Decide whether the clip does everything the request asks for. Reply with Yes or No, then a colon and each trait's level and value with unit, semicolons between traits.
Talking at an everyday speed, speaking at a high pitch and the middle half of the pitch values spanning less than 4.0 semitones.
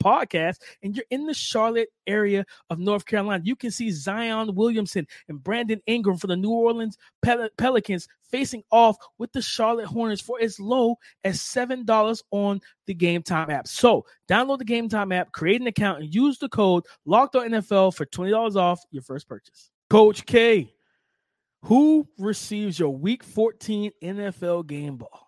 Yes: average, 170 wpm; high, 215 Hz; average, 3.4 semitones